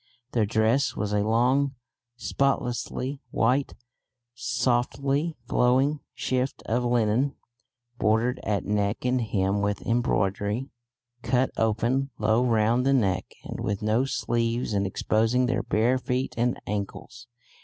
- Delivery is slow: Yes, slow, 125 wpm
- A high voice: No, low, 120 Hz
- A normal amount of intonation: Yes, average, 3.1 semitones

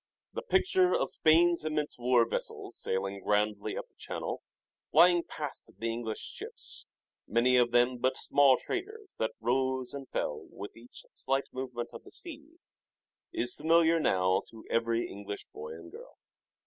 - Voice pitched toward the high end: No, low, 125 Hz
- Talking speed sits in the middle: Yes, average, 155 wpm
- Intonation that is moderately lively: No, wide, 6.5 semitones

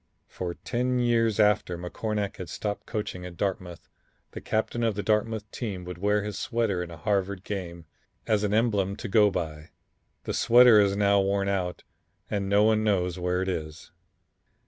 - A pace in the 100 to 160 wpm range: No, average, 175 wpm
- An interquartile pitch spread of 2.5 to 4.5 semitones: Yes, average, 3.0 semitones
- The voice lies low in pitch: Yes, low, 100 Hz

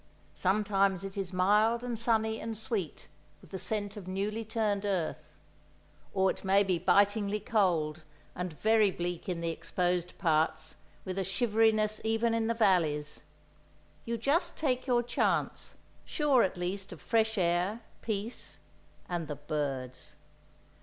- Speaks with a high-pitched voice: Yes, high, 200 Hz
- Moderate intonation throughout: Yes, average, 3.8 semitones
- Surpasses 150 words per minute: No, average, 145 wpm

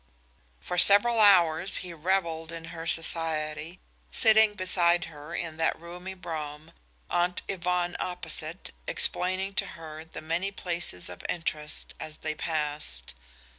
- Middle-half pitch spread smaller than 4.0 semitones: Yes, narrow, 2.5 semitones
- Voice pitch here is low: No, medium, 170 Hz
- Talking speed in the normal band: No, slow, 130 wpm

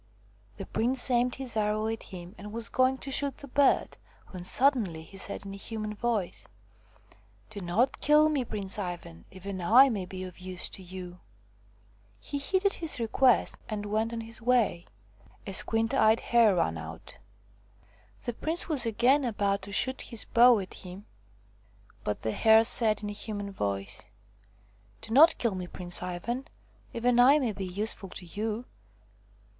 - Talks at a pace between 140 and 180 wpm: Yes, average, 170 wpm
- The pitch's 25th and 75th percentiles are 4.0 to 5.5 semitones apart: Yes, average, 4.9 semitones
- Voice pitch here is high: Yes, high, 215 Hz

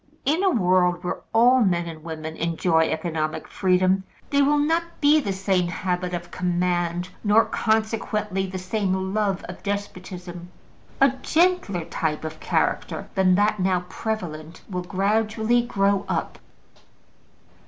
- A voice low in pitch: No, high, 190 Hz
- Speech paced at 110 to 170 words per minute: Yes, slow, 135 wpm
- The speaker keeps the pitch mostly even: No, average, 3.7 semitones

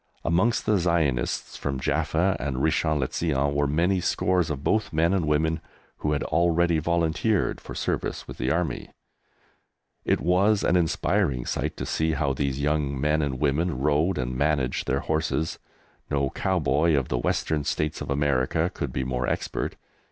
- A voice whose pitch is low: Yes, very low, 75 Hz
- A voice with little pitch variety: No, average, 3.4 semitones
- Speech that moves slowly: No, average, 165 wpm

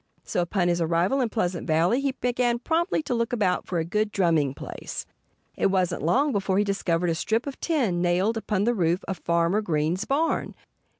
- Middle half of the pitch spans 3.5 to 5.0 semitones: No, wide, 5.5 semitones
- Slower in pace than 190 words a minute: No, average, 195 wpm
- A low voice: No, high, 195 Hz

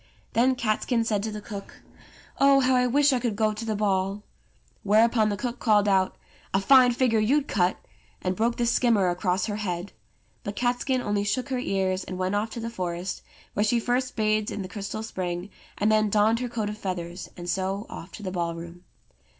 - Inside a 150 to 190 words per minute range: No, fast, 205 wpm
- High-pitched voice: Yes, high, 210 Hz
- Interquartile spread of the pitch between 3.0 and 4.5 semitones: Yes, average, 3.8 semitones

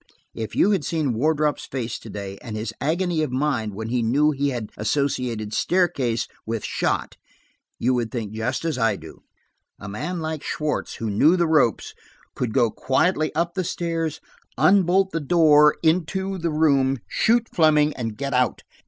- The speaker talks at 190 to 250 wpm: No, average, 170 wpm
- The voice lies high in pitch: No, medium, 145 Hz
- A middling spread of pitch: No, wide, 6.2 semitones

